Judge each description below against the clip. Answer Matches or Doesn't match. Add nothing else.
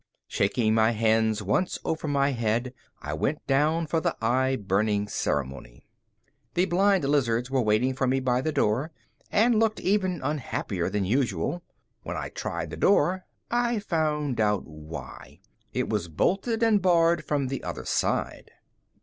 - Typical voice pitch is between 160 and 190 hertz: Doesn't match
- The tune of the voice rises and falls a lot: Matches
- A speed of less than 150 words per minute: Doesn't match